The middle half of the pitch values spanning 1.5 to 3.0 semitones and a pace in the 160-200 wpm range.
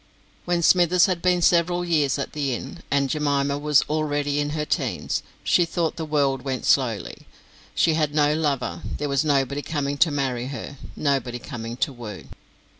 Yes: narrow, 2.5 semitones; average, 175 wpm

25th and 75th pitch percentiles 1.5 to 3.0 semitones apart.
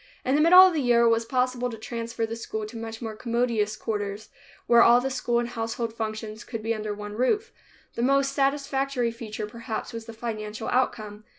Yes: narrow, 2.4 semitones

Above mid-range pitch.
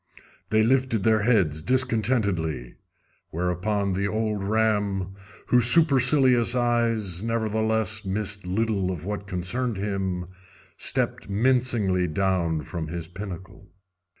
No: low, 105 Hz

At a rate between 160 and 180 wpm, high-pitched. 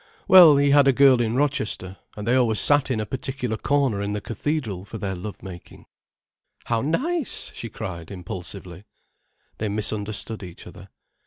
No: average, 165 wpm; low, 110 Hz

